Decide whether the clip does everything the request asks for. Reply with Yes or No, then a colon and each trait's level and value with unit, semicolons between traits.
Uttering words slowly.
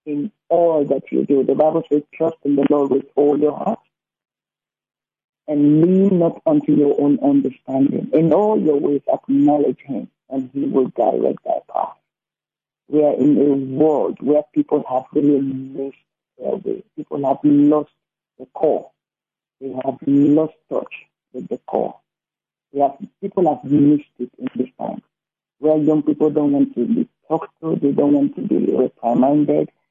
No: average, 165 wpm